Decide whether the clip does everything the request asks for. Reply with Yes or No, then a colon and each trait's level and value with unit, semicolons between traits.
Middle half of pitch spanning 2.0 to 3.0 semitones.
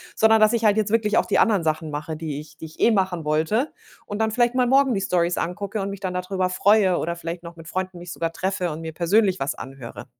No: average, 4.5 semitones